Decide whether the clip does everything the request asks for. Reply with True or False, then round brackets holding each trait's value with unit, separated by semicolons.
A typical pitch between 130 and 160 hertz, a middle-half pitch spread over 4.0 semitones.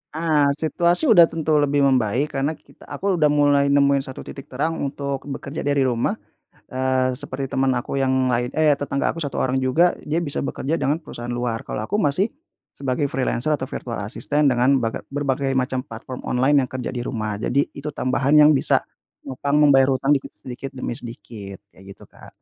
False (135 Hz; 2.4 semitones)